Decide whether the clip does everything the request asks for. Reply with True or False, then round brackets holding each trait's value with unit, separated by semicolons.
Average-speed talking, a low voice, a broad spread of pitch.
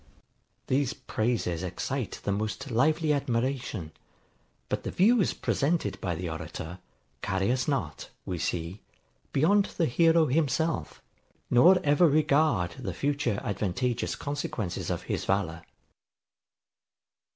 False (115 wpm; 125 Hz; 7.8 semitones)